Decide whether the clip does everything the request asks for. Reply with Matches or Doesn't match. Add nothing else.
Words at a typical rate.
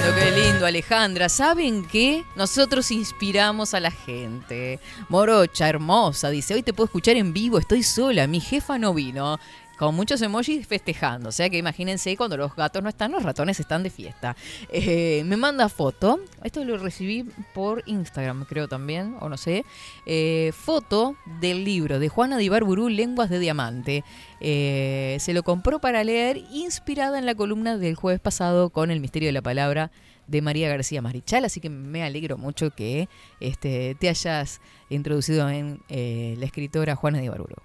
Matches